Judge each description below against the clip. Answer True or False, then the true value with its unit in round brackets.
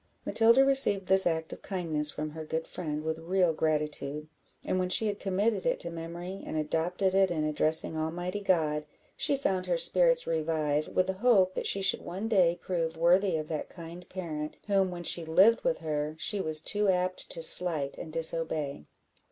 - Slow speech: False (190 wpm)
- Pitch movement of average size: True (3.4 semitones)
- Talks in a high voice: False (170 Hz)